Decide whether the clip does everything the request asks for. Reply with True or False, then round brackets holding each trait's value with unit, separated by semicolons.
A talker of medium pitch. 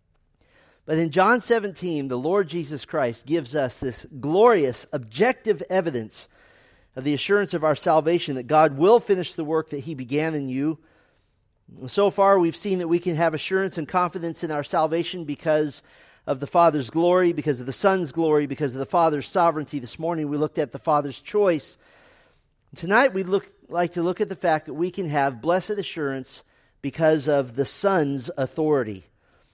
True (160 Hz)